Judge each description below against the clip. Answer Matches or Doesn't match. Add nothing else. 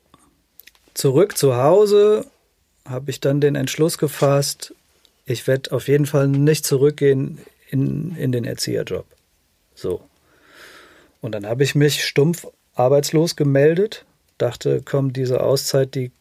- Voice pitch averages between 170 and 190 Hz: Doesn't match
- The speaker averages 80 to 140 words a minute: Matches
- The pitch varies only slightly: Matches